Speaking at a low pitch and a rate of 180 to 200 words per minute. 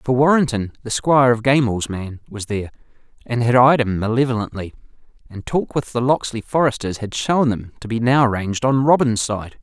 Yes: low, 120 Hz; average, 185 wpm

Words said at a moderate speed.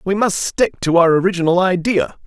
Yes: average, 185 wpm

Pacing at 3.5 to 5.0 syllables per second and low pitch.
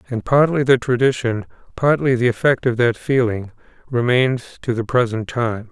Yes: 4.8 syllables/s; low, 120 Hz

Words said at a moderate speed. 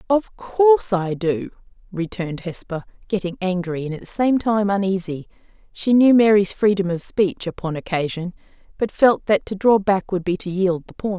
Yes: average, 180 wpm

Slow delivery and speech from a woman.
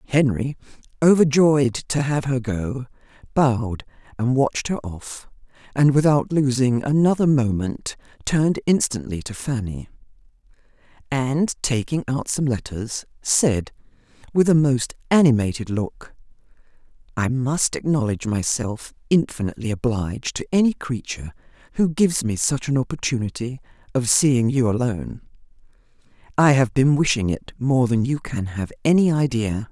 Yes: slow, 125 wpm; female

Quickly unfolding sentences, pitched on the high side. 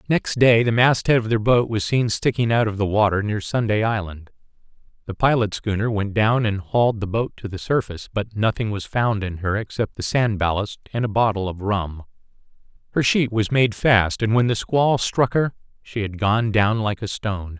No: fast, 210 wpm; low, 110 Hz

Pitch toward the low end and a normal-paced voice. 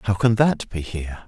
No: low, 105 Hz; fast, 235 wpm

